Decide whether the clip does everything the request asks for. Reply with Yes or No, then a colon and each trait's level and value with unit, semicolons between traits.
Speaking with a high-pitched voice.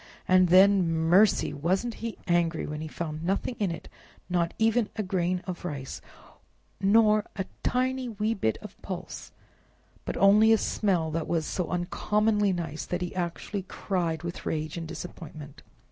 No: medium, 180 Hz